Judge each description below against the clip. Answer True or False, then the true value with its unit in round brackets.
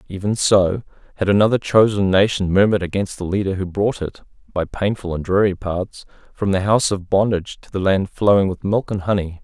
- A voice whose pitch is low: True (100 Hz)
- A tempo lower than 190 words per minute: False (195 wpm)